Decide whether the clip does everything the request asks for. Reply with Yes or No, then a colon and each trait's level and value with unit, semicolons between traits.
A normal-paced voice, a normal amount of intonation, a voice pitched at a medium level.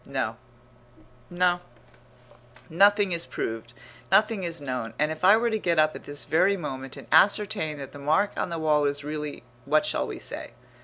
Yes: average, 185 wpm; average, 4.5 semitones; medium, 155 Hz